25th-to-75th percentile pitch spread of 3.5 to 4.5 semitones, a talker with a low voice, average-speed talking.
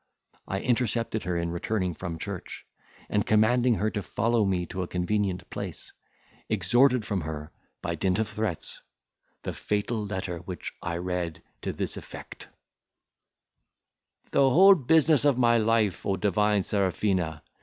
Yes: average, 4.2 semitones; low, 105 Hz; average, 145 wpm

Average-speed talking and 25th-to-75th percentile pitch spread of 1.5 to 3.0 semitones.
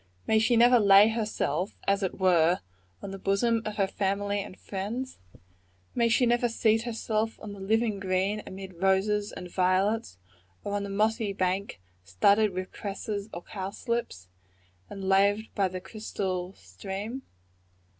Yes: average, 150 wpm; narrow, 2.5 semitones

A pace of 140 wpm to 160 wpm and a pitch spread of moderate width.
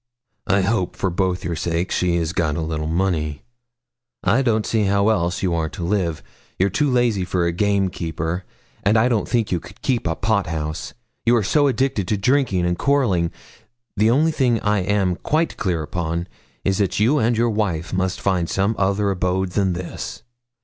No: average, 195 wpm; average, 4.2 semitones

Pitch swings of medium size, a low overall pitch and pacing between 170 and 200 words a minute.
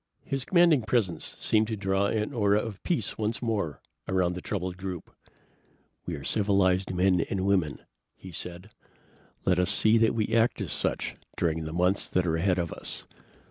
Yes: average, 3.3 semitones; very low, 95 Hz; average, 180 wpm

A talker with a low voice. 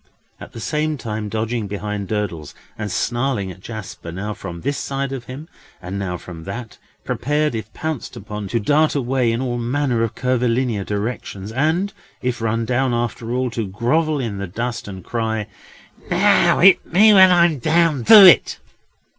Yes: low, 120 Hz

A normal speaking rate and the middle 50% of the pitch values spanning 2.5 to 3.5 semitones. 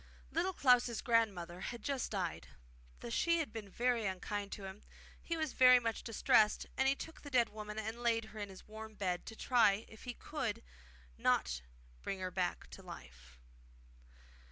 No: average, 180 wpm; average, 4.3 semitones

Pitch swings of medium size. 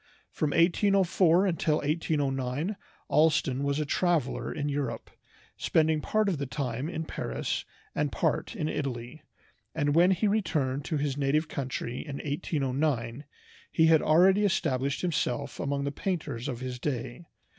Yes: average, 3.5 semitones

